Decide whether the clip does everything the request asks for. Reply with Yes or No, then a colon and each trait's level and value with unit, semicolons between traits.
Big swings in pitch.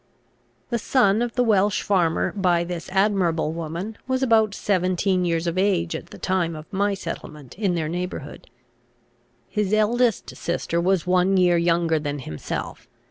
No: average, 3.4 semitones